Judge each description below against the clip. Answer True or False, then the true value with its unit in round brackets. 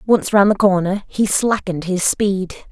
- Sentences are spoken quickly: False (175 wpm)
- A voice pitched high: True (195 Hz)